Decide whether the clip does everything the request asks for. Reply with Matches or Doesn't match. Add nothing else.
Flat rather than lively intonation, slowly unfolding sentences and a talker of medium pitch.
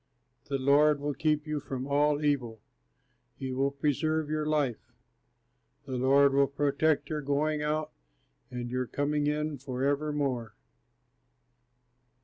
Matches